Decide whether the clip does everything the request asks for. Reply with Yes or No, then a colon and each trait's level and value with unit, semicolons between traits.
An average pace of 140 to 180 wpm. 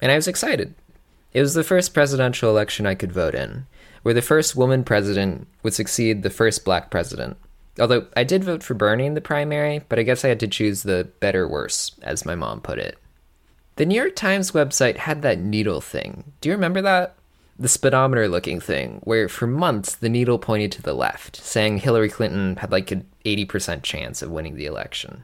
No: average, 200 wpm